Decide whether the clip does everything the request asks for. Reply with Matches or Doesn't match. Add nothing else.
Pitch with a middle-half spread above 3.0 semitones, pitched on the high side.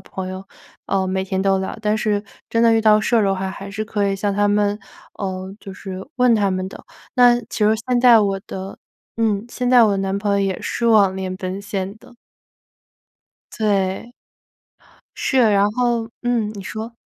Doesn't match